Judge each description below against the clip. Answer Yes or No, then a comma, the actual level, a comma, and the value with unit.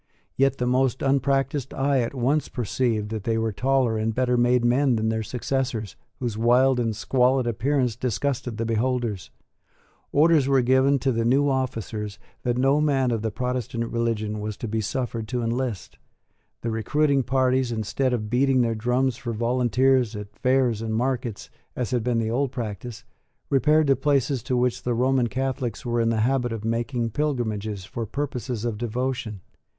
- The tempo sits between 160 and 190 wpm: Yes, average, 175 wpm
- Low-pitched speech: Yes, low, 125 Hz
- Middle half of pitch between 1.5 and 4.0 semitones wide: Yes, average, 2.7 semitones